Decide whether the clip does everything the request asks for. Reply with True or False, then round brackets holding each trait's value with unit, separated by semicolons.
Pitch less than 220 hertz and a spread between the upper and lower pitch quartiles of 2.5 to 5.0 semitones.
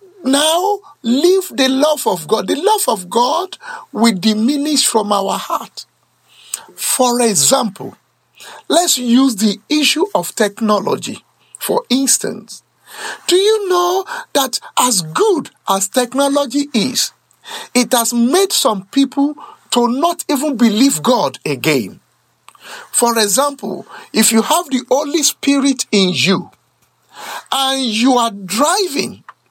False (270 Hz; 4.7 semitones)